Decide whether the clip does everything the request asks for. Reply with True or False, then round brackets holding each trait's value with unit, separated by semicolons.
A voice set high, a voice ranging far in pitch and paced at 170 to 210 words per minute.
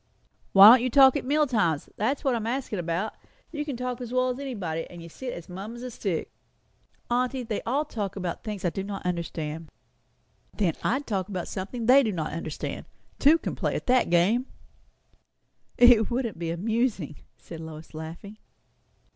True (215 Hz; 6.5 semitones; 185 wpm)